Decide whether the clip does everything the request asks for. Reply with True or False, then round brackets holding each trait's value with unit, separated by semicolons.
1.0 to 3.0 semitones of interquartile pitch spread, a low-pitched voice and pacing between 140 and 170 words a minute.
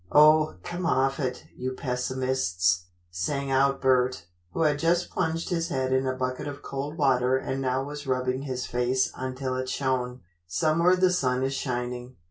True (2.4 semitones; 130 Hz; 165 wpm)